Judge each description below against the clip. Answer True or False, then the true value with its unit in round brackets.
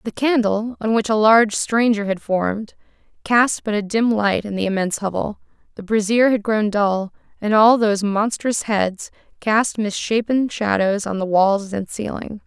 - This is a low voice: False (215 Hz)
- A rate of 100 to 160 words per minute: False (175 wpm)